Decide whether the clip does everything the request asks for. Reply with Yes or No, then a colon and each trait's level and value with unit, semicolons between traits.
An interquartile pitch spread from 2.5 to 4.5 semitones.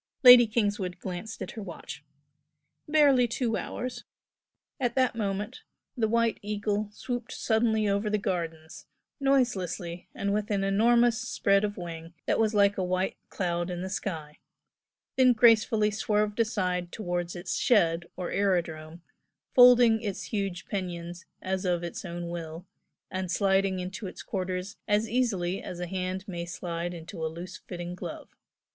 Yes: average, 3.8 semitones